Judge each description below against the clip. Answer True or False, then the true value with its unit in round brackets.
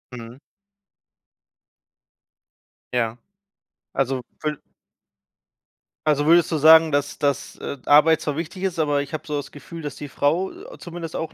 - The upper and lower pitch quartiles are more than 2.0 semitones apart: True (2.5 semitones)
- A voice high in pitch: False (150 Hz)